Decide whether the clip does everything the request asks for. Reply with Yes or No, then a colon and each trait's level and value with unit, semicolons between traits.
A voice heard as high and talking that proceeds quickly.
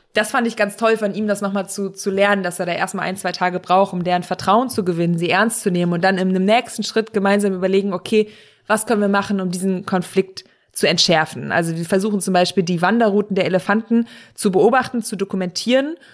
Yes: high, 195 Hz; fast, 220 wpm